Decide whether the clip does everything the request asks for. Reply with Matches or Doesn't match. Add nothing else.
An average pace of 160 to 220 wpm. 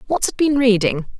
Matches